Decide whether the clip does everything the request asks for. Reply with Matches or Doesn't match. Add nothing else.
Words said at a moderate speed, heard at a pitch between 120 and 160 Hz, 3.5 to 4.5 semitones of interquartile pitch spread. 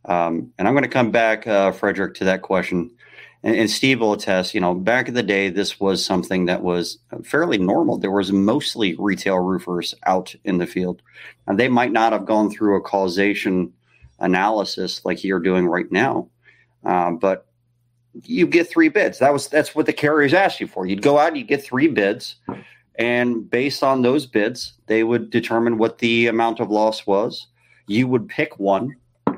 Doesn't match